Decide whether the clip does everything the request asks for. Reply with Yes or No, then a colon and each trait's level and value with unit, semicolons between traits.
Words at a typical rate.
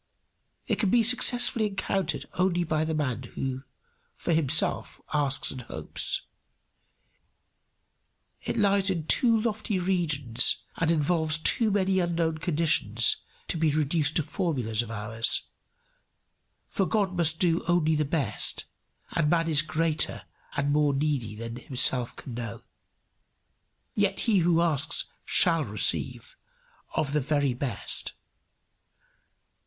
No: slow, 125 wpm